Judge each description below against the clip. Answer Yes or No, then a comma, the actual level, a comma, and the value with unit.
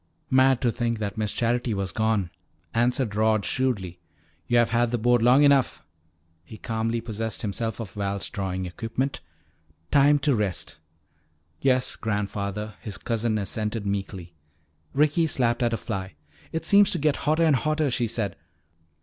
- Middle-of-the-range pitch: No, low, 115 Hz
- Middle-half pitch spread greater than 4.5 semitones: No, average, 3.9 semitones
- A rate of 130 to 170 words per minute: Yes, average, 150 wpm